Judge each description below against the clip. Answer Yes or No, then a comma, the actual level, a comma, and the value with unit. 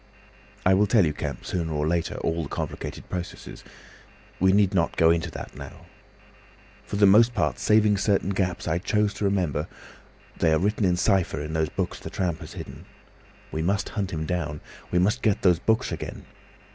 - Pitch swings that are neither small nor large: Yes, average, 3.8 semitones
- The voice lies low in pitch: Yes, very low, 90 Hz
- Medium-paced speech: Yes, average, 190 wpm